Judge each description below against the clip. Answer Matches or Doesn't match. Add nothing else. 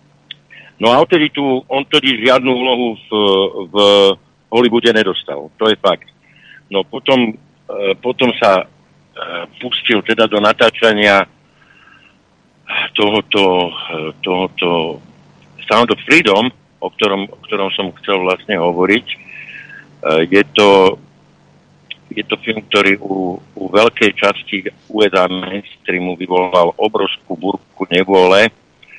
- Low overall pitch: Matches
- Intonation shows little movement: Doesn't match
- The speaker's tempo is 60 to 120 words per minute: Matches